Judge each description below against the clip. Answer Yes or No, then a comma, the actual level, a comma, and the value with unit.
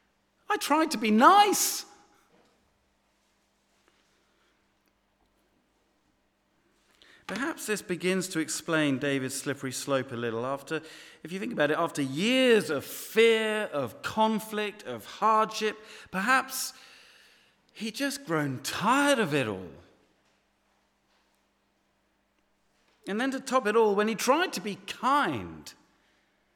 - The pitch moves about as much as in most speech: No, wide, 8.8 semitones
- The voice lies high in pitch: Yes, high, 215 Hz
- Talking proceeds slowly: Yes, slow, 110 wpm